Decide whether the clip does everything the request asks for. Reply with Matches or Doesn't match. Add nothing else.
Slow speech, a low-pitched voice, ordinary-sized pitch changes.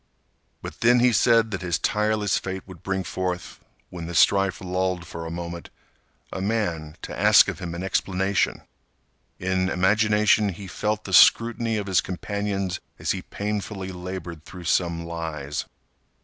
Doesn't match